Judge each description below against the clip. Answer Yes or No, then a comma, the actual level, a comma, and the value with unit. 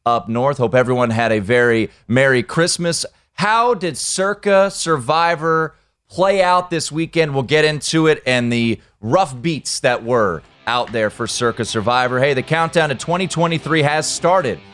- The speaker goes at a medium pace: Yes, average, 160 wpm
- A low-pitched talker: No, medium, 155 Hz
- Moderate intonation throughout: No, wide, 5.8 semitones